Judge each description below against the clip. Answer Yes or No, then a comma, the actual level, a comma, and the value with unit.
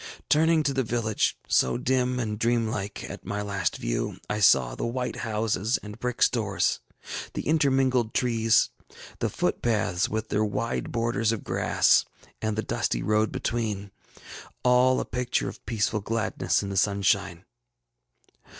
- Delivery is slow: No, average, 150 wpm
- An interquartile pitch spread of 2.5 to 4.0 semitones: Yes, average, 3.3 semitones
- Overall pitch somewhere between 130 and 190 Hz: No, low, 110 Hz